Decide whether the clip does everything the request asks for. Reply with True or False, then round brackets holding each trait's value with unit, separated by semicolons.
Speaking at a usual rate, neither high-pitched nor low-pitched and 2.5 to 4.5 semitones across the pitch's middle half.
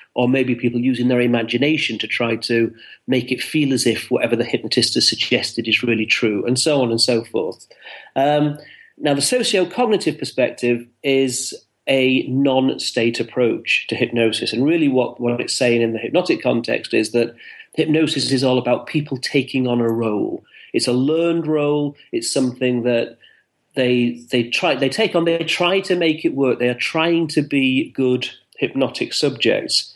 False (175 wpm; 130 Hz; 3.8 semitones)